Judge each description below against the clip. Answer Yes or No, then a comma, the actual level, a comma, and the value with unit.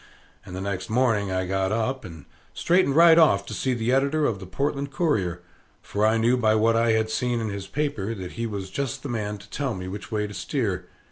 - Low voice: Yes, low, 110 Hz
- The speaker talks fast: Yes, fast, 230 wpm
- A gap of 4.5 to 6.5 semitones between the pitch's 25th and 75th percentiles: Yes, average, 5.1 semitones